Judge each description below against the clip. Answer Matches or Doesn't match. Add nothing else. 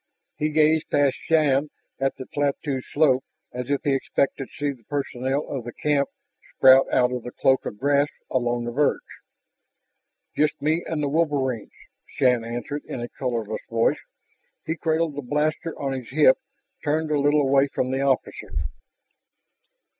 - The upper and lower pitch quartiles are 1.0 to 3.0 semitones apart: Matches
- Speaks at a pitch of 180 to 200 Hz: Doesn't match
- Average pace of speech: Matches